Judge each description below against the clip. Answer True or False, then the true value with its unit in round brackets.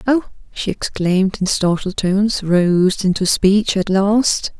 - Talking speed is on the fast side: False (145 wpm)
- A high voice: True (195 Hz)